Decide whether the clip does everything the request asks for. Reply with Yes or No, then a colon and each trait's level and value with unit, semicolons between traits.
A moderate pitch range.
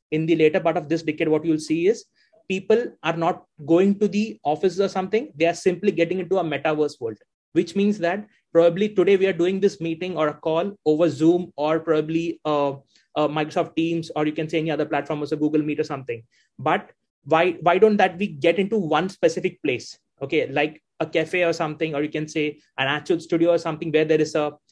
Yes: average, 3.3 semitones